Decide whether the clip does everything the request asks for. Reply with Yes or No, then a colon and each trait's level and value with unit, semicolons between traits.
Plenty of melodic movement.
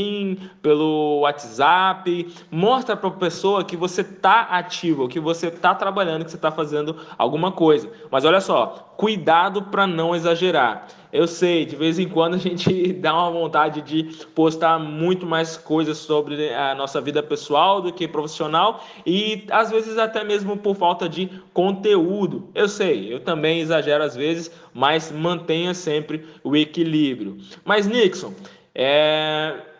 No: average, 3.2 semitones